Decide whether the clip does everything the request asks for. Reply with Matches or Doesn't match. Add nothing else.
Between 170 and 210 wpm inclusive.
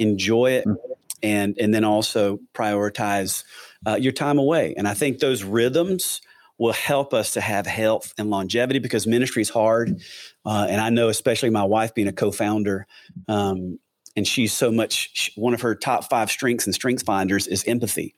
Matches